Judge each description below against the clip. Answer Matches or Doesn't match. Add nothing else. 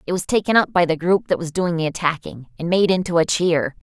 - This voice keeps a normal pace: Doesn't match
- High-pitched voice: Doesn't match